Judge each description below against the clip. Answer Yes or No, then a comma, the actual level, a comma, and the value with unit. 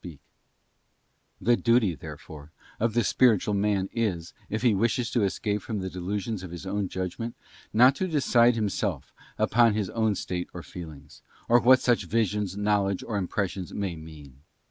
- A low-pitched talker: Yes, low, 105 Hz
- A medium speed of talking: Yes, average, 165 wpm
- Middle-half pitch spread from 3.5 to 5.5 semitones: Yes, average, 4.2 semitones